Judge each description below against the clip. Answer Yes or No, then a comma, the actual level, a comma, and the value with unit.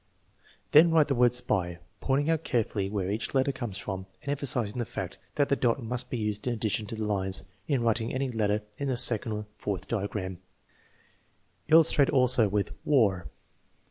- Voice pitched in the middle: No, low, 115 Hz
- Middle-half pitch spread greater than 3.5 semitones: Yes, average, 4.5 semitones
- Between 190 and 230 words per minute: Yes, average, 195 wpm